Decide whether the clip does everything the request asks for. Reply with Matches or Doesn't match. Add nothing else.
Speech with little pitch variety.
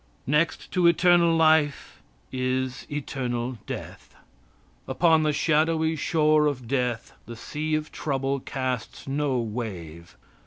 Doesn't match